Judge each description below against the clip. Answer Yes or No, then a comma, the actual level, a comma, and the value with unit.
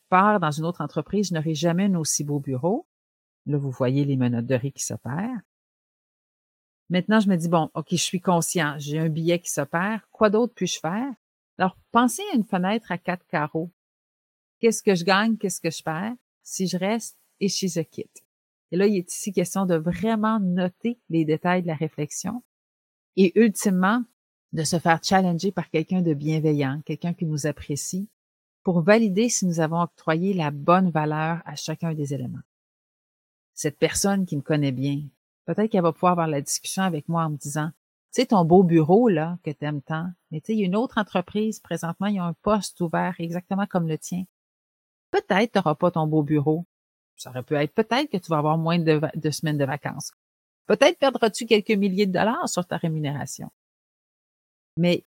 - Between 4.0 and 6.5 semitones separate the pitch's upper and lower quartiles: Yes, average, 4.3 semitones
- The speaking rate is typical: Yes, average, 200 wpm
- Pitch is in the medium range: Yes, medium, 175 Hz